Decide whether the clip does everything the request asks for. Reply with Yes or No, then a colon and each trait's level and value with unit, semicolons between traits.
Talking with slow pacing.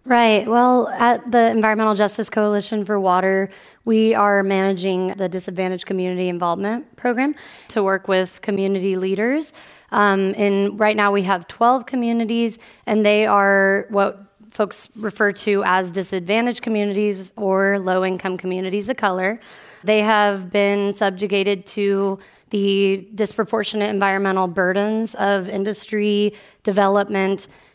Yes: slow, 125 wpm